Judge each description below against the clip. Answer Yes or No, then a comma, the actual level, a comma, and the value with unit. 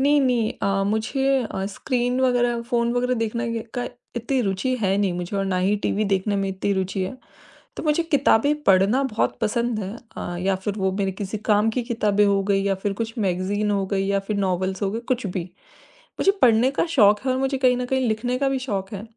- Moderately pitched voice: No, high, 215 Hz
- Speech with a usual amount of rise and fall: Yes, average, 4.3 semitones